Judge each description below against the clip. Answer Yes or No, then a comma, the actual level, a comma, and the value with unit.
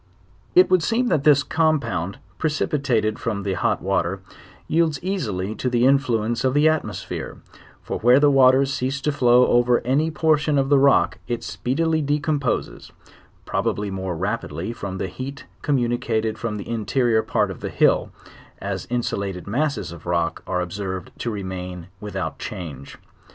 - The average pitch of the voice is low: Yes, low, 120 Hz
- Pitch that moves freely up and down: Yes, wide, 6.5 semitones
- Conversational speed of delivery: Yes, average, 160 wpm